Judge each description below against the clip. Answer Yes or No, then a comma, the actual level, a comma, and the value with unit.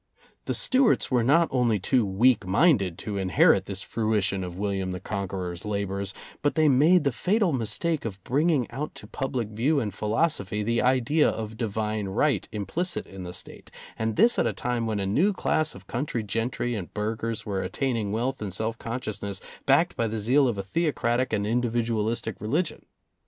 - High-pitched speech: No, low, 115 Hz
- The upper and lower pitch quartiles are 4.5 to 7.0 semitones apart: Yes, average, 4.9 semitones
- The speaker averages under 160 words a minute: No, average, 185 wpm